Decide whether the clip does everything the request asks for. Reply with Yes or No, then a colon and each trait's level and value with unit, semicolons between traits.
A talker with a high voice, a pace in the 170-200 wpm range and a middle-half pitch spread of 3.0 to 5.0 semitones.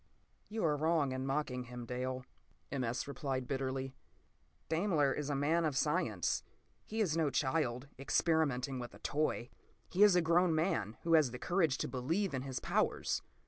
No: medium, 140 Hz; average, 180 wpm; average, 4.0 semitones